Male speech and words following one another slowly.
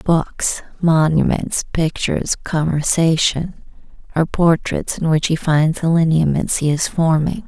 No: female; slow, 120 wpm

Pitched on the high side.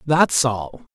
No: low, 130 Hz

